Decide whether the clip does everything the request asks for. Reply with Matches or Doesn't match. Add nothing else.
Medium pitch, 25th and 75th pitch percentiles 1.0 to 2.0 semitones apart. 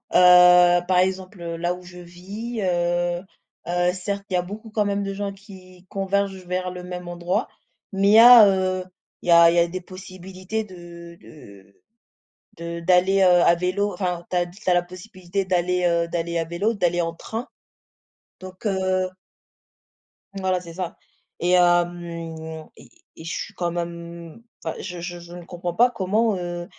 Matches